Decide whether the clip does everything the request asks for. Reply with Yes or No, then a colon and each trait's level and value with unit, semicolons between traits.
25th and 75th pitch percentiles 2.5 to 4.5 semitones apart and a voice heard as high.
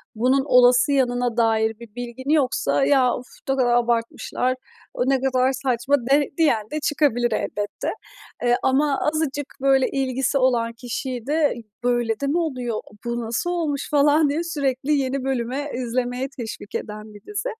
Yes: average, 2.9 semitones; very high, 255 Hz